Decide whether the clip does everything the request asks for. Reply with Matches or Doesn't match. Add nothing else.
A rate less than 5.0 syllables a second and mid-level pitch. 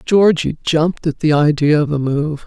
Matches